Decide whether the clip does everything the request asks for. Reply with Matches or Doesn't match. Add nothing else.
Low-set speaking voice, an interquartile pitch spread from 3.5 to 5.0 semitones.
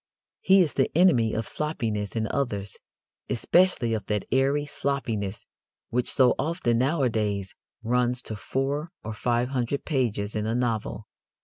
Matches